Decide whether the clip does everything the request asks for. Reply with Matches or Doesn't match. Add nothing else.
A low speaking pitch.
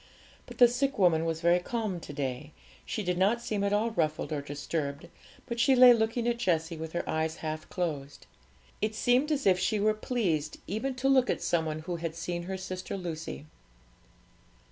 Doesn't match